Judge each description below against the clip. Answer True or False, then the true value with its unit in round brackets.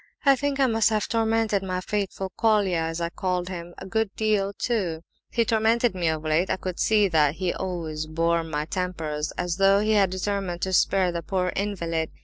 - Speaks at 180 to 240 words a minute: True (200 wpm)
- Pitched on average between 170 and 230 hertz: True (185 Hz)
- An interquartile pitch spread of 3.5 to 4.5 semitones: True (3.9 semitones)